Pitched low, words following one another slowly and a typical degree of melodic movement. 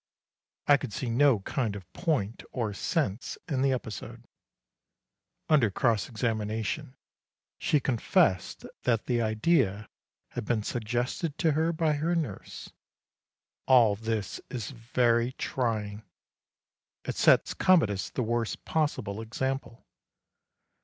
Yes: low, 120 Hz; slow, 115 wpm; average, 4.4 semitones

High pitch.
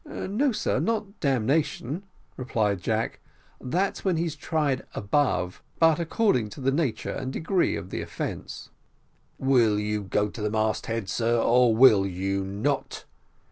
No: low, 125 Hz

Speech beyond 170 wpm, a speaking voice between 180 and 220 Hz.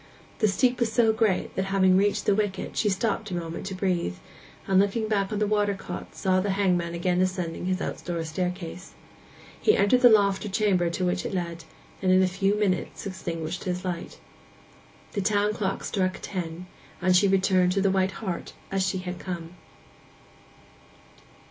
Yes: average, 185 wpm; high, 190 Hz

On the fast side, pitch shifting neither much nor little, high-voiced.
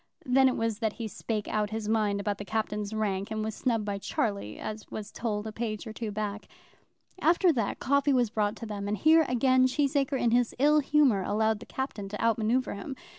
Yes: fast, 220 wpm; average, 3.6 semitones; high, 220 Hz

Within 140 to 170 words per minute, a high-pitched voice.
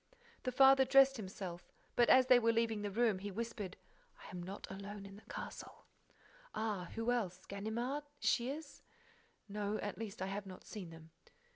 Yes: average, 165 wpm; high, 210 Hz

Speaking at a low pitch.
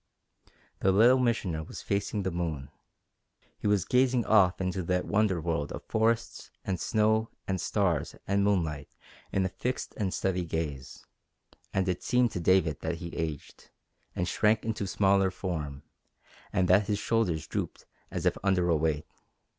Yes: very low, 95 Hz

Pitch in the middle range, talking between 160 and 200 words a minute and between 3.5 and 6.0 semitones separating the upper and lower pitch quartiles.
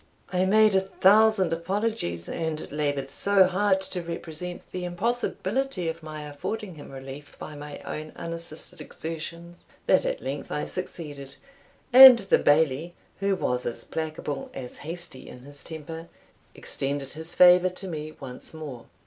No: medium, 165 Hz; average, 150 wpm; average, 4.3 semitones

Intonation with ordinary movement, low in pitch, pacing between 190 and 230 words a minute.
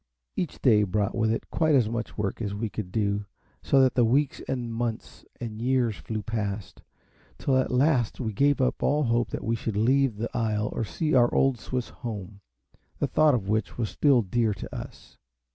Yes: average, 3.4 semitones; low, 115 Hz; average, 195 wpm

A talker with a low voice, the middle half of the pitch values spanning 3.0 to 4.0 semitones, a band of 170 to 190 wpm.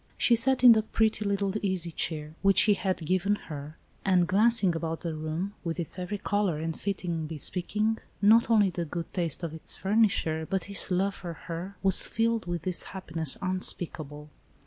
No: medium, 185 Hz; average, 3.7 semitones; average, 180 wpm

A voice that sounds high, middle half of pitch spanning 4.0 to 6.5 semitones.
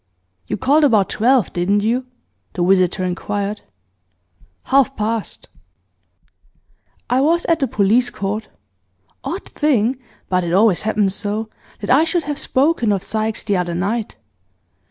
Yes: high, 220 Hz; average, 5.0 semitones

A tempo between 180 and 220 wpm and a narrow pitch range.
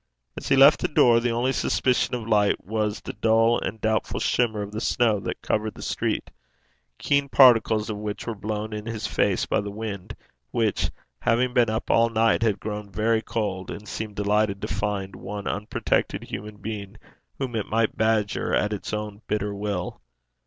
Yes: average, 185 wpm; narrow, 1.8 semitones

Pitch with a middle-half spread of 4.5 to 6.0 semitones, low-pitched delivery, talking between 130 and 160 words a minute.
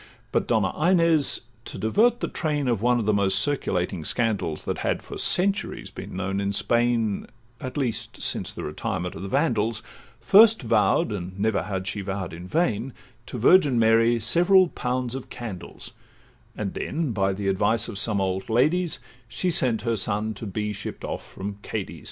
No: average, 5.1 semitones; low, 115 Hz; average, 175 wpm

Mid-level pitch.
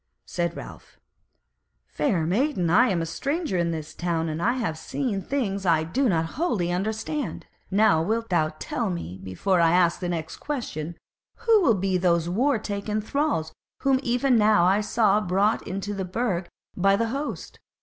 No: high, 195 Hz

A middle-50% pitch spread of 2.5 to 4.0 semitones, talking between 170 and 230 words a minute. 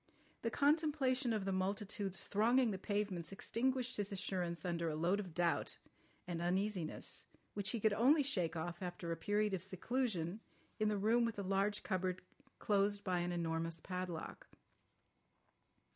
No: average, 3.7 semitones; average, 155 wpm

